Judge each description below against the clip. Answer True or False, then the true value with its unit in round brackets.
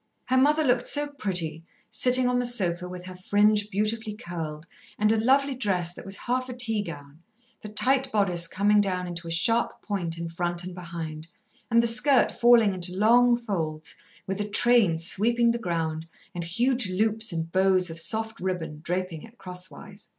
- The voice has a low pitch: False (200 Hz)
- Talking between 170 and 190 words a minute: True (180 wpm)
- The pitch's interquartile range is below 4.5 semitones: False (5.3 semitones)